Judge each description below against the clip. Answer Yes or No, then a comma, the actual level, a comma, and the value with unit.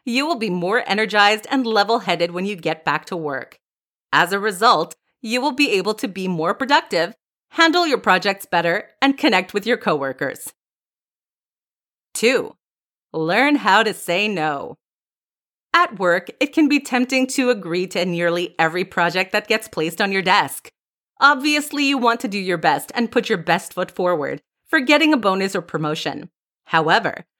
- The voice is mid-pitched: No, high, 205 Hz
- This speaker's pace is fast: No, average, 170 wpm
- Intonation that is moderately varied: No, wide, 7.0 semitones